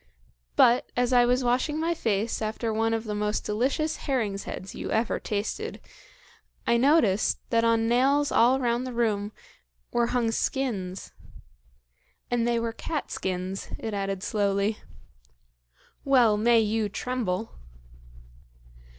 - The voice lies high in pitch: Yes, high, 230 Hz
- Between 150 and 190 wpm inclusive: No, slow, 135 wpm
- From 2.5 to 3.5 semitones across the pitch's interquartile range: Yes, average, 3.0 semitones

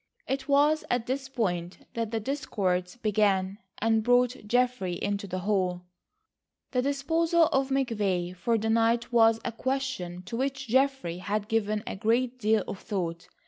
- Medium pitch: No, high, 225 Hz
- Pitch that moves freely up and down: No, average, 5.0 semitones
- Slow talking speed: No, average, 155 wpm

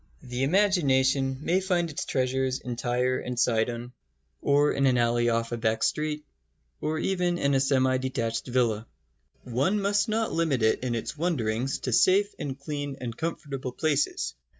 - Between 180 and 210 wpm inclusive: No, average, 165 wpm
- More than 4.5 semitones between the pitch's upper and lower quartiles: No, average, 4.2 semitones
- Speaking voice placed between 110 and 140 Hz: Yes, low, 135 Hz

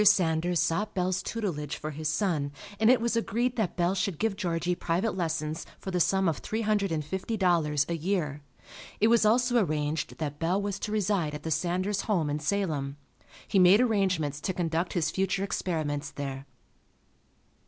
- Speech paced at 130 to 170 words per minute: No, average, 180 wpm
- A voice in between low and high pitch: Yes, medium, 180 Hz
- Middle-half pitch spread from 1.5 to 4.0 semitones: No, average, 4.5 semitones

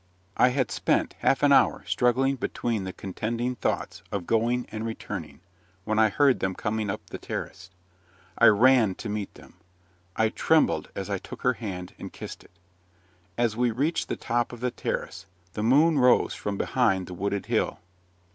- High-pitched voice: No, low, 115 Hz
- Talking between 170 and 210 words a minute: Yes, average, 175 wpm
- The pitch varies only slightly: No, average, 3.7 semitones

